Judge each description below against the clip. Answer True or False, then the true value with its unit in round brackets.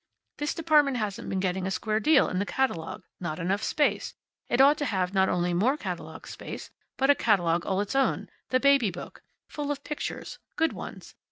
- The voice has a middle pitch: False (220 Hz)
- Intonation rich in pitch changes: True (7.0 semitones)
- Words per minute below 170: False (195 wpm)